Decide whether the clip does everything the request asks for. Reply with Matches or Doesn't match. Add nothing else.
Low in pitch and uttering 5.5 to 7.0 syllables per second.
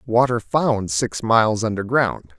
Doesn't match